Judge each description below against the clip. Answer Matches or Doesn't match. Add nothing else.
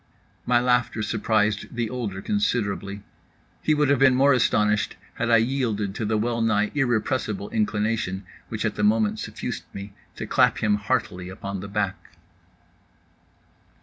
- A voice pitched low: Matches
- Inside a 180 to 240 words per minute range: Doesn't match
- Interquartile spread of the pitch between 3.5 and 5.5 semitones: Doesn't match